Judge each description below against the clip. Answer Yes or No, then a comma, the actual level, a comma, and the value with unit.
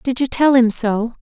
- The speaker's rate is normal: No, fast, 245 wpm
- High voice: Yes, high, 245 Hz